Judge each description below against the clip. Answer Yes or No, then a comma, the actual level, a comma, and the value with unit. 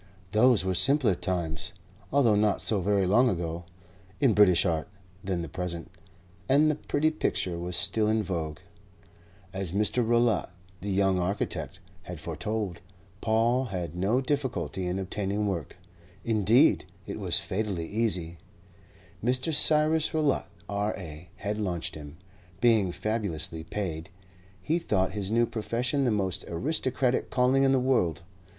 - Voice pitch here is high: No, low, 100 Hz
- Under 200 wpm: Yes, average, 140 wpm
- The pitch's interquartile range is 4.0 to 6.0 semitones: Yes, average, 5.3 semitones